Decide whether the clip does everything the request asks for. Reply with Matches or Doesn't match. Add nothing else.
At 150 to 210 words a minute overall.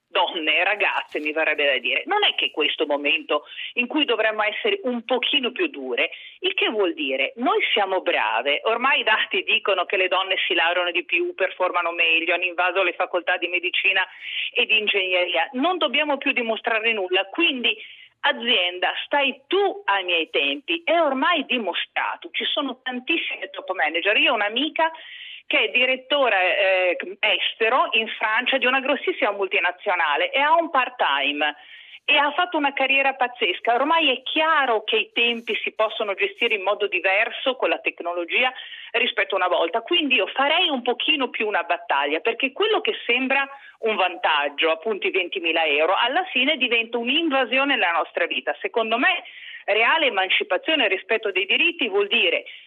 Matches